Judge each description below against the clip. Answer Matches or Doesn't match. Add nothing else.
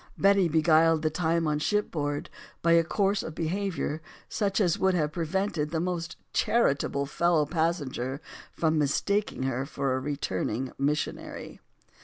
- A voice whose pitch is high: Doesn't match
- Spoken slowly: Doesn't match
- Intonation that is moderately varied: Matches